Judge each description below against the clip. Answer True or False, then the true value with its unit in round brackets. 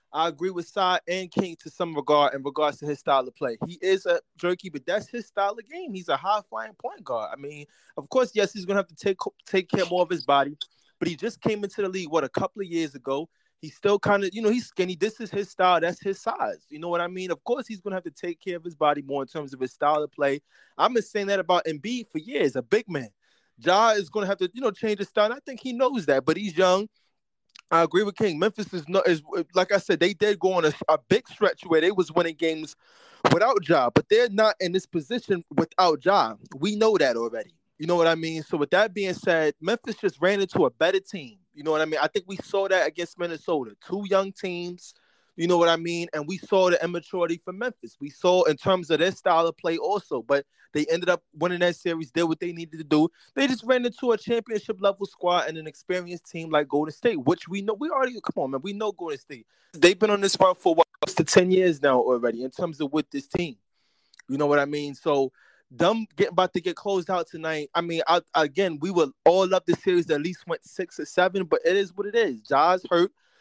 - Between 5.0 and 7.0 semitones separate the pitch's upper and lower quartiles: False (3.9 semitones)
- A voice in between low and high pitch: True (180 Hz)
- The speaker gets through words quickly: True (265 wpm)